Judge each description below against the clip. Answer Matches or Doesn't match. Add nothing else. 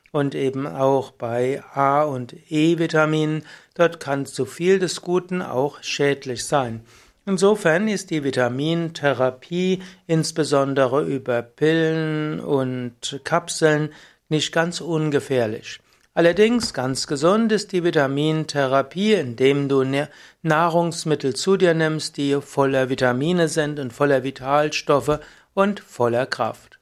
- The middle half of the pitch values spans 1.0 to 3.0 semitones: Doesn't match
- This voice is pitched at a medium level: Matches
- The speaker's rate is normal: Doesn't match